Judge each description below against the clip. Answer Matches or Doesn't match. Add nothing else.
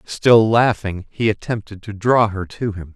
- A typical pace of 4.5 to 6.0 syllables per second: Doesn't match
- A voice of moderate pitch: Doesn't match